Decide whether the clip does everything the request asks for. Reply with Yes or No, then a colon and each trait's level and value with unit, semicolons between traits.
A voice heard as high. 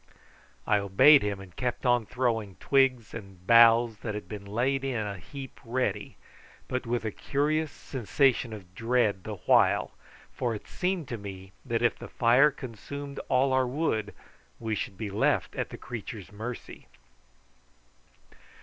No: low, 115 Hz